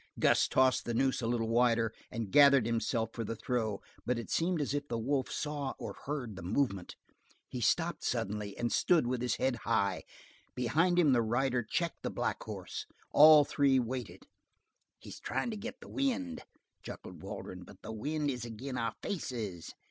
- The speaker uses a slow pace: No, average, 180 wpm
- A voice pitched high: No, low, 125 Hz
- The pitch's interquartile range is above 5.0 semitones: No, average, 4.2 semitones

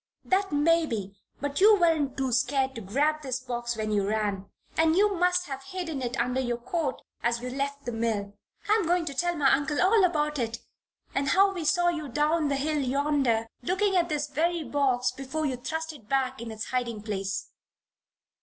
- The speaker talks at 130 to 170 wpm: No, average, 200 wpm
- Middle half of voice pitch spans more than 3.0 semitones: Yes, average, 5.1 semitones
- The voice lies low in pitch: No, very high, 280 Hz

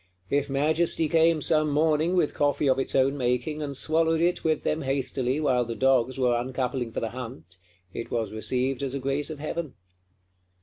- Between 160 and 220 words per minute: Yes, average, 185 wpm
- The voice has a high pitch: No, low, 135 Hz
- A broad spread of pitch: No, average, 3.6 semitones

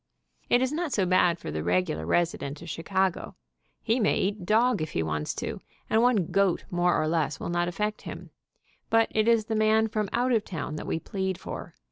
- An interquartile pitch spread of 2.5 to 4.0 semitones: No, average, 5.1 semitones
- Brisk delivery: Yes, fast, 215 wpm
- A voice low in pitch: No, high, 190 Hz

